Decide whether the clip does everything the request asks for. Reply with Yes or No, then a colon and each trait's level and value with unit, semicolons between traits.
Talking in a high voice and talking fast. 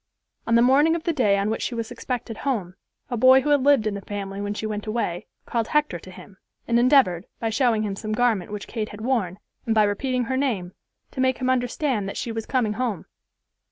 Yes: high, 225 Hz; fast, 230 wpm